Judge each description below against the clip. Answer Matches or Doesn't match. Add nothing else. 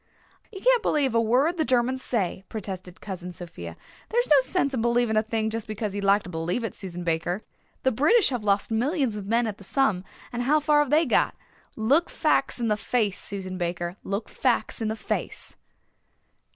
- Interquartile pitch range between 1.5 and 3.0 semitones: Doesn't match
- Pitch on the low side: Doesn't match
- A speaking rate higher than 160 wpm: Matches